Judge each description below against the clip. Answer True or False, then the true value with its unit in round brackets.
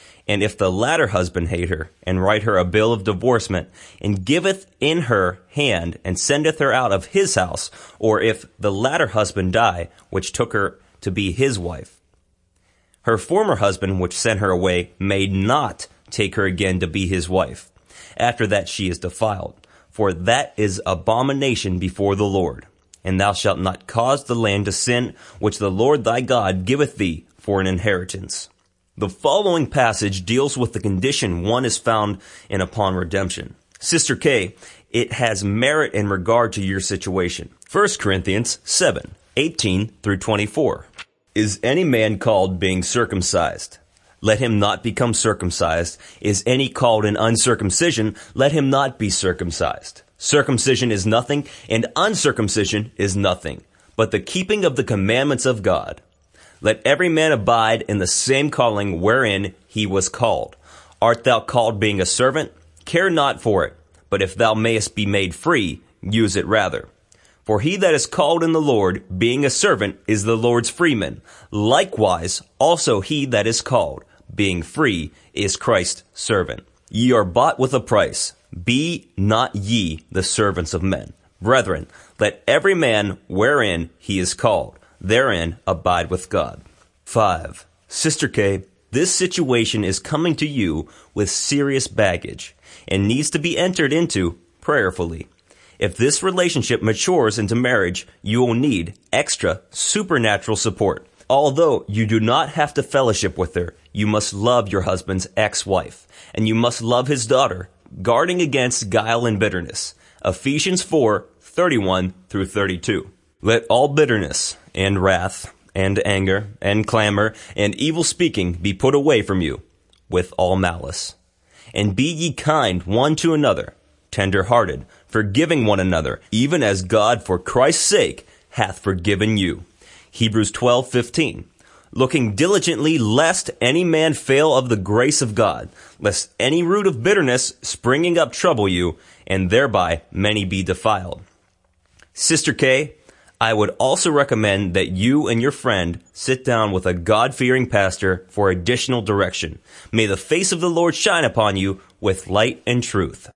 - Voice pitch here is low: True (105 Hz)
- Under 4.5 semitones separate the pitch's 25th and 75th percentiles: False (4.8 semitones)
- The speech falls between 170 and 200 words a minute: False (155 wpm)